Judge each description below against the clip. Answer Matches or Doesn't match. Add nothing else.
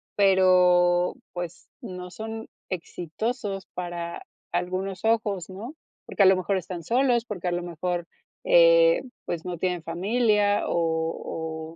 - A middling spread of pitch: Matches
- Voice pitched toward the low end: Doesn't match